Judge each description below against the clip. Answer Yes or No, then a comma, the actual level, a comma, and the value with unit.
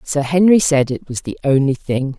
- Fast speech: Yes, fast, 220 wpm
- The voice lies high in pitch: No, medium, 145 Hz